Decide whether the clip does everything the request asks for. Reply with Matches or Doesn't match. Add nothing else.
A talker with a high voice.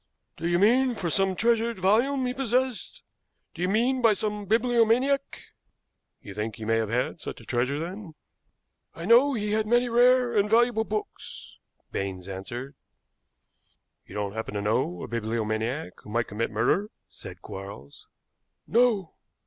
Matches